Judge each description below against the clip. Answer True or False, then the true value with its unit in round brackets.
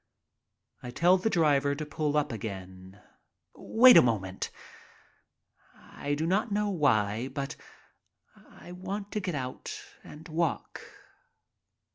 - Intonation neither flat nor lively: False (7.0 semitones)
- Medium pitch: True (150 Hz)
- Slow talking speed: True (120 wpm)